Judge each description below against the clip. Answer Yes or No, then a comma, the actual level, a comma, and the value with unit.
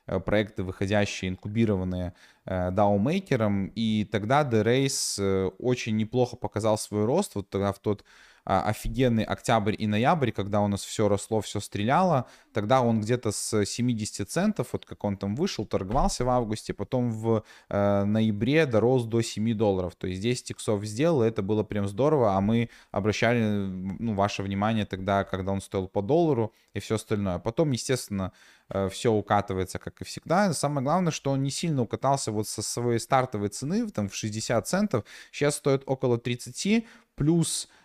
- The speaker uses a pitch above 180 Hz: No, low, 110 Hz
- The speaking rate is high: Yes, fast, 165 wpm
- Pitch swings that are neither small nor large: Yes, average, 3.7 semitones